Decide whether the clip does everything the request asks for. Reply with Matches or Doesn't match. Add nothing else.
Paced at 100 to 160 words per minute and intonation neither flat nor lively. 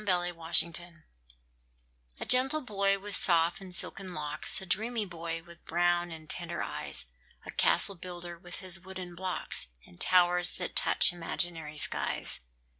Doesn't match